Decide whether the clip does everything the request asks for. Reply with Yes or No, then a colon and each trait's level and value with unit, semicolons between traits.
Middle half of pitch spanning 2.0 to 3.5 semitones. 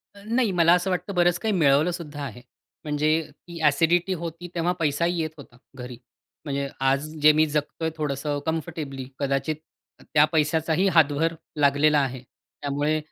Yes: average, 2.9 semitones